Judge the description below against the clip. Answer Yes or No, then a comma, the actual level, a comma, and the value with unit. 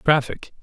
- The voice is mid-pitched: Yes, medium, 145 Hz